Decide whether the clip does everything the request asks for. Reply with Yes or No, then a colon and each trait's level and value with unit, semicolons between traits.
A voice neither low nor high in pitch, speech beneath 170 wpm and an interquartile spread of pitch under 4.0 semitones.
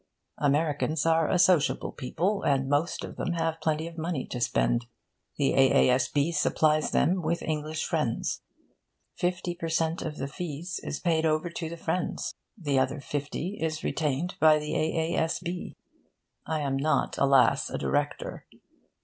Yes: medium, 155 Hz; average, 150 wpm; average, 2.7 semitones